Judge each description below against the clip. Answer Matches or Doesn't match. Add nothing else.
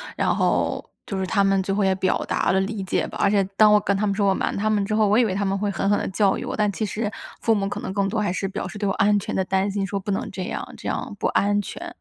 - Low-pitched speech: Doesn't match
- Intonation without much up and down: Matches